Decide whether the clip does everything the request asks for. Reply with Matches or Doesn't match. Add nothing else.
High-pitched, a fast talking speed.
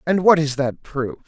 Doesn't match